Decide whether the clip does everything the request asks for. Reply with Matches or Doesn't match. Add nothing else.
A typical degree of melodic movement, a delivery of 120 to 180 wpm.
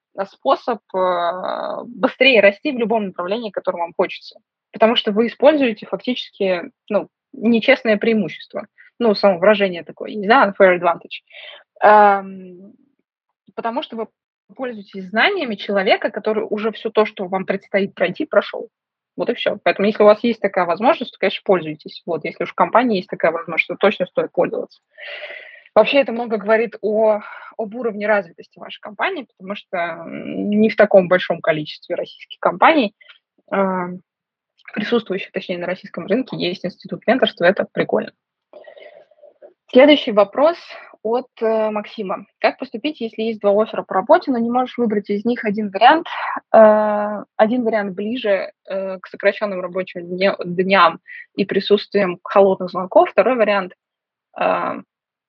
Matches